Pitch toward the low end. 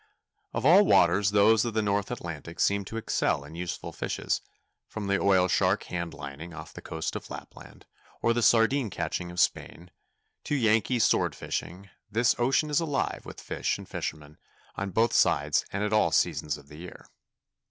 Yes: low, 100 Hz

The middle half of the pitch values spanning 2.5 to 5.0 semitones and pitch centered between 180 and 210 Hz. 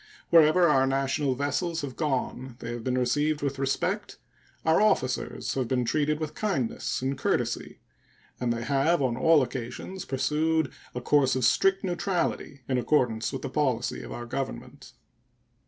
No: average, 3.4 semitones; low, 135 Hz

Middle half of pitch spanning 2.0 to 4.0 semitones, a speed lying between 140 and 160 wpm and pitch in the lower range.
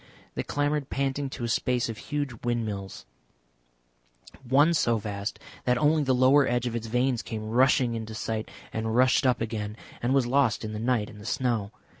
No: average, 3.2 semitones; average, 185 wpm; low, 120 Hz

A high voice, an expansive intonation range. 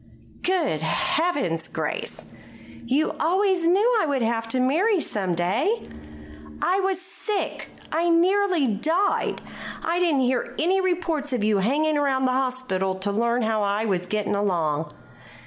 Yes: very high, 270 Hz; wide, 8.9 semitones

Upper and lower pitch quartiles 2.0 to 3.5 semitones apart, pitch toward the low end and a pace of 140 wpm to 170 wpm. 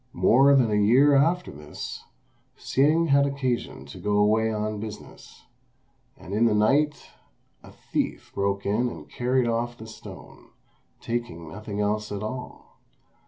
No: average, 4.3 semitones; low, 115 Hz; average, 145 wpm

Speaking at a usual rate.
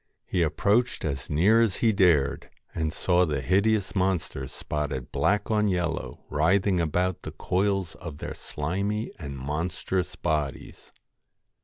Yes: average, 155 wpm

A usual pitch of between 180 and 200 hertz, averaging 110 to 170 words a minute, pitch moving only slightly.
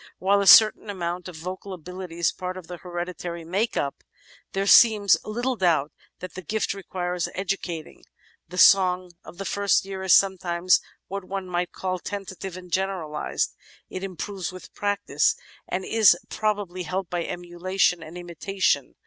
Yes: medium, 185 Hz; average, 155 wpm; narrow, 1.9 semitones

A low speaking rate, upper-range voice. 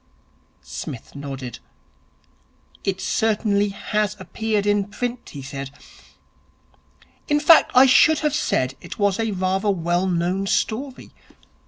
Yes: slow, 120 wpm; high, 200 Hz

